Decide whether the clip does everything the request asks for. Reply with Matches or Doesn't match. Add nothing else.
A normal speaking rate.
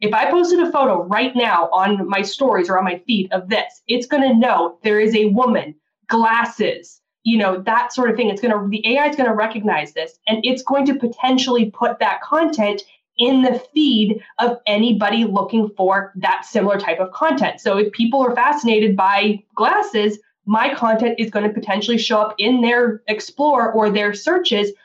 Matches